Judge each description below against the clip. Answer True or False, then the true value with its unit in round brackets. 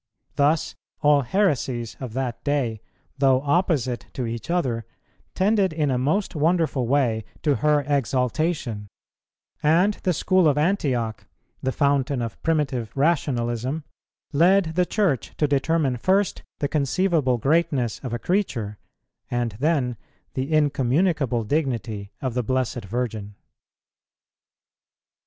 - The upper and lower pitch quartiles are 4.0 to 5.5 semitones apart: True (4.8 semitones)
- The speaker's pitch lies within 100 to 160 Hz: True (140 Hz)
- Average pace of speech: False (120 wpm)